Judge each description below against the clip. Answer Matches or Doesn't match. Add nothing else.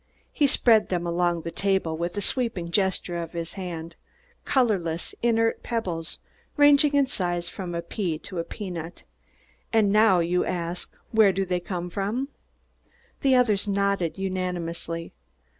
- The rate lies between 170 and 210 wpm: Doesn't match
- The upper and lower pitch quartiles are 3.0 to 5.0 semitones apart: Matches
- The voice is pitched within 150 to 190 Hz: Matches